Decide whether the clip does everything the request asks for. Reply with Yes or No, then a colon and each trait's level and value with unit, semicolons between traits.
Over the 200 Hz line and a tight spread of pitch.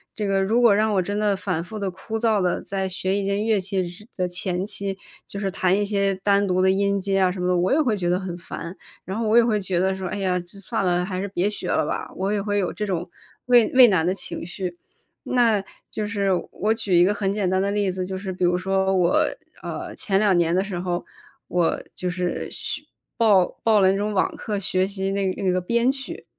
No: high, 195 Hz; narrow, 2.1 semitones